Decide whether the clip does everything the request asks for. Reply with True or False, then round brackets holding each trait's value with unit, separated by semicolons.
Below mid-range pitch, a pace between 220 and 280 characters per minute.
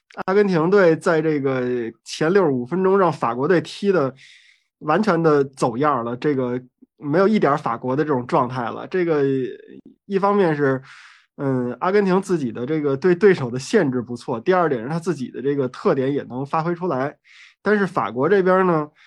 False (155 Hz; 275 characters per minute)